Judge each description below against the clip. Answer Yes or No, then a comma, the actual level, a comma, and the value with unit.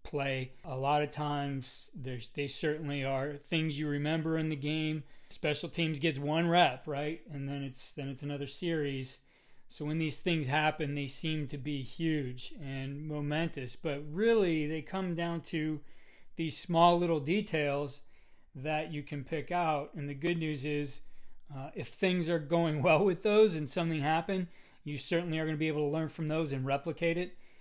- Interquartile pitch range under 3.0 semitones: Yes, narrow, 2.4 semitones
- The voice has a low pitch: No, medium, 155 Hz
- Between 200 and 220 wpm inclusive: No, average, 185 wpm